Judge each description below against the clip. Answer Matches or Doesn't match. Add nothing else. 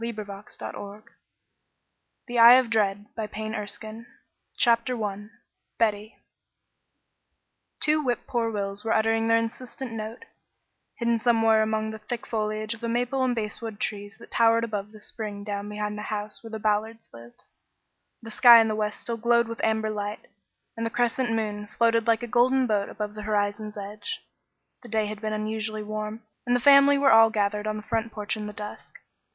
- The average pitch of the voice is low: Doesn't match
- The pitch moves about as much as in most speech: Doesn't match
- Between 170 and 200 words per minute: Matches